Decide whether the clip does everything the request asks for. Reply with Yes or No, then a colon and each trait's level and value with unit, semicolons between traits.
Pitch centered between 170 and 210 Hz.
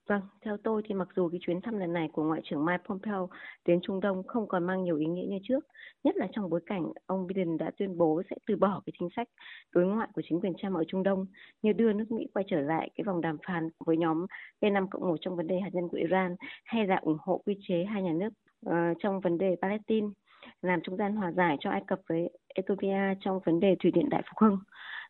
Yes: high, 190 Hz